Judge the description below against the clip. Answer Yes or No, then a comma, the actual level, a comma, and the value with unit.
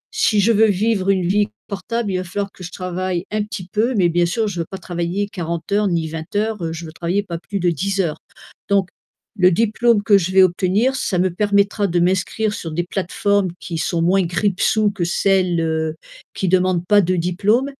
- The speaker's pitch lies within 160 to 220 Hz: Yes, medium, 185 Hz